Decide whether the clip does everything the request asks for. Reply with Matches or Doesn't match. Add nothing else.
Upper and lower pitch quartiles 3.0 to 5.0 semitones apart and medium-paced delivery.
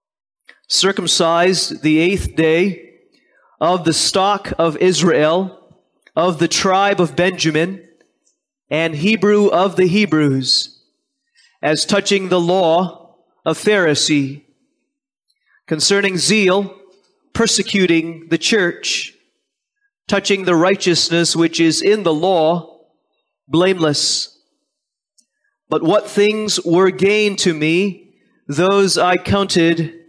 Doesn't match